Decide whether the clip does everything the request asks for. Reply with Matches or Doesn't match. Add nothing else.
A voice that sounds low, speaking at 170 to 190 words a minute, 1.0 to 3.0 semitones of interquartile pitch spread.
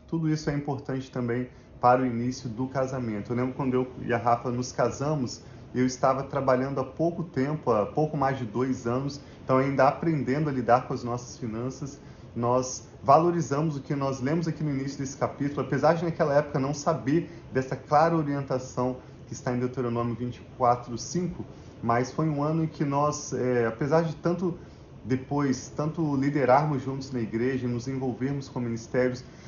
Matches